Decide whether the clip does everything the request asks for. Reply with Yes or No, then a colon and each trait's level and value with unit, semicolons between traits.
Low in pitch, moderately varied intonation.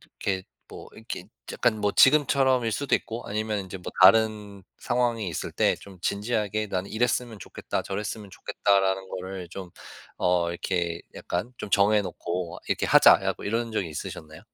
Yes: low, 100 Hz; average, 3.1 semitones